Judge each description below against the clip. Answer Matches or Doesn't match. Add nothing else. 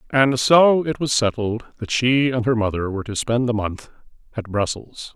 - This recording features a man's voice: Matches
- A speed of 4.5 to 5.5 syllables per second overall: Matches